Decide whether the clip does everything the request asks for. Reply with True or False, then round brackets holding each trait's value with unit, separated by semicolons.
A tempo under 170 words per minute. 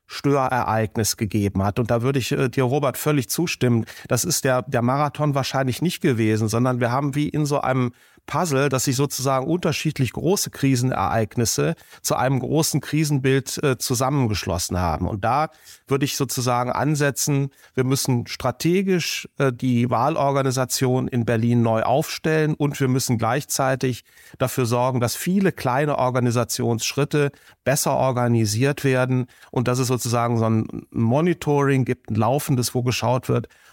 True (150 wpm)